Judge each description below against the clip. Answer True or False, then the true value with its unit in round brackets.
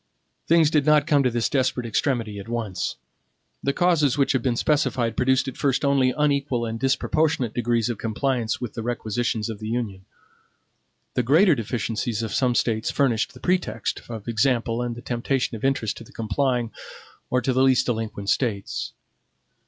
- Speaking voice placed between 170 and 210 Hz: False (120 Hz)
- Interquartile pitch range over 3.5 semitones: False (3.2 semitones)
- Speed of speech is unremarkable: True (175 wpm)